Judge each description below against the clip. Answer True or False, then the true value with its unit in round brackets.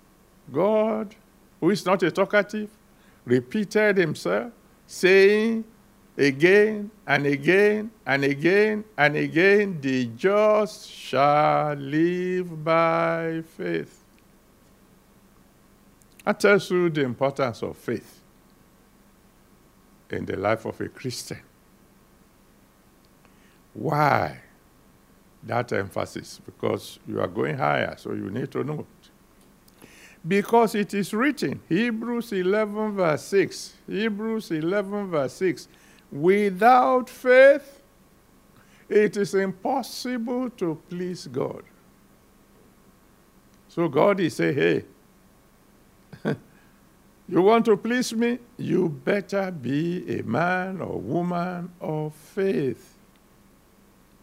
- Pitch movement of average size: True (4.7 semitones)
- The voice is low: False (195 Hz)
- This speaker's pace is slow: True (95 wpm)